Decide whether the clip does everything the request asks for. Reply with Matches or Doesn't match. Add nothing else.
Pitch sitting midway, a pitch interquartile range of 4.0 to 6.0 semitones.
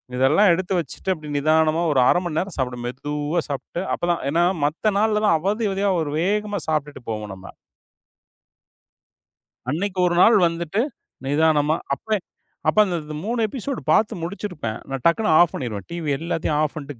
Matches